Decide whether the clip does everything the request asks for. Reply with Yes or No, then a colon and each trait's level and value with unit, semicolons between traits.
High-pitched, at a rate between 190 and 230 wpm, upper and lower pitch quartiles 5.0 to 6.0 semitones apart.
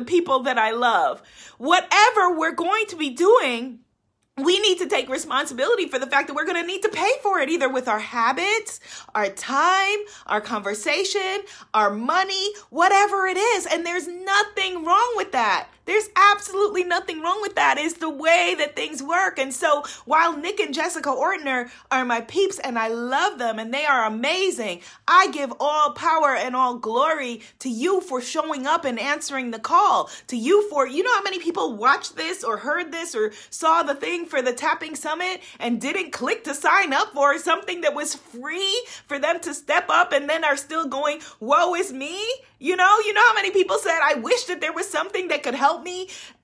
Yes: very high, 325 Hz; average, 200 wpm; wide, 5.6 semitones